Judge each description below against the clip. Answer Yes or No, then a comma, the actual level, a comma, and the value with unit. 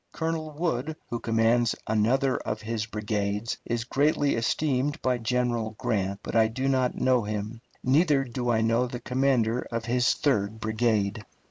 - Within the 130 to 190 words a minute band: Yes, average, 155 wpm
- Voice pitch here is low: Yes, low, 120 Hz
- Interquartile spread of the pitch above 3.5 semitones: No, average, 2.8 semitones